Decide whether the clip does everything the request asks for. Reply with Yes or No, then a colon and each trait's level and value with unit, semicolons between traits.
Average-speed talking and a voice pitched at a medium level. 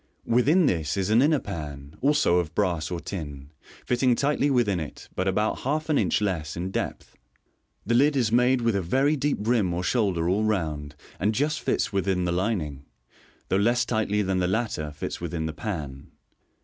No: average, 190 wpm; low, 100 Hz